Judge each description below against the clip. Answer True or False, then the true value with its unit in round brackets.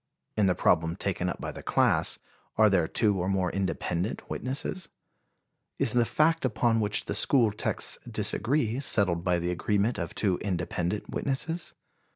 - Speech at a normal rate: True (160 wpm)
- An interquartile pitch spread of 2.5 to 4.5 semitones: False (5.2 semitones)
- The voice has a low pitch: True (105 Hz)